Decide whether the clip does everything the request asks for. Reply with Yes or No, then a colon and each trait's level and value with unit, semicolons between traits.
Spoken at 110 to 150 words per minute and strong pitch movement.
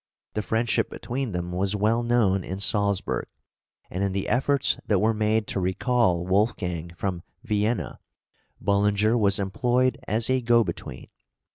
No: average, 145 wpm; average, 3.6 semitones